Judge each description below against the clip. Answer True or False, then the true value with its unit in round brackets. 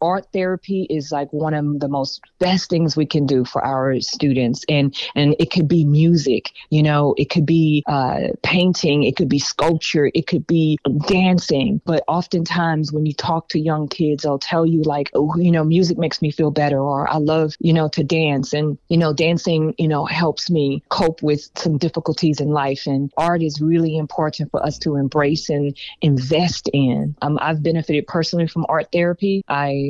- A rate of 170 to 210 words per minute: True (195 wpm)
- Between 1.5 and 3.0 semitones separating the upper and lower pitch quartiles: True (2.5 semitones)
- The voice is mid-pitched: True (155 Hz)